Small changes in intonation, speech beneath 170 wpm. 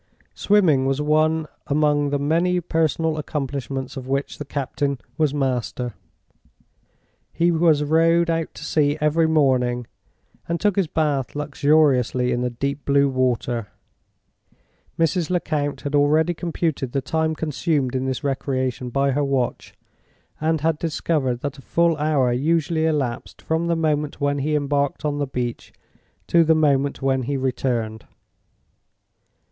No: average, 3.1 semitones; average, 140 wpm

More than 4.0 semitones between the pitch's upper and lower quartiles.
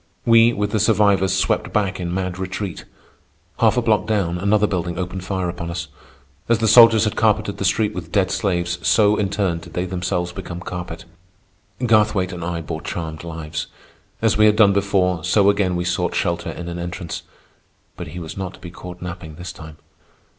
No: average, 2.8 semitones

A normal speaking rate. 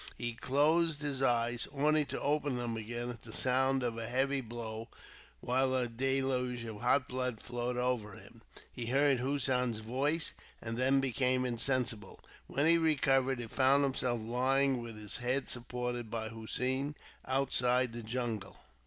Yes: average, 155 wpm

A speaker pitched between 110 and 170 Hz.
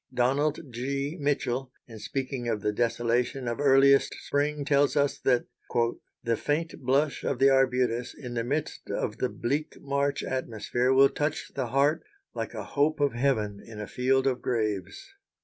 Yes: low, 135 Hz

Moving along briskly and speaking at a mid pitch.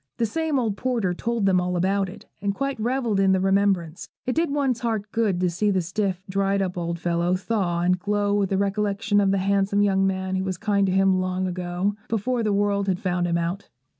No: fast, 225 wpm; high, 195 Hz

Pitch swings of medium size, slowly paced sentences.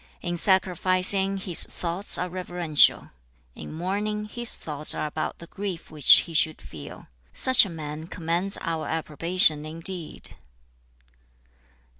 Yes: average, 3.2 semitones; slow, 125 wpm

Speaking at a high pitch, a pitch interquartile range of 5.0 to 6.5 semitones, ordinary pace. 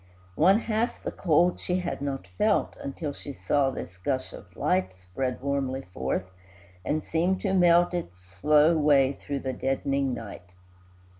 No: medium, 140 Hz; wide, 5.4 semitones; average, 155 wpm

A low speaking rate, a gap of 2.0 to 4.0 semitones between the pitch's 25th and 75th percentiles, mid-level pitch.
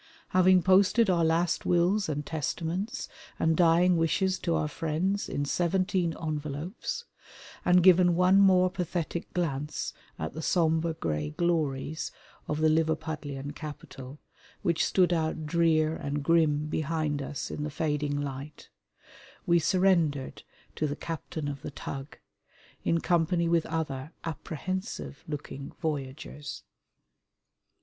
Yes: slow, 125 wpm; average, 3.1 semitones; medium, 160 Hz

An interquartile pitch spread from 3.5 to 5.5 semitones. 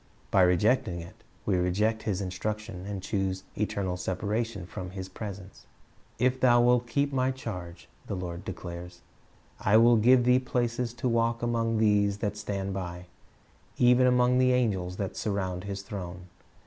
Yes: average, 4.4 semitones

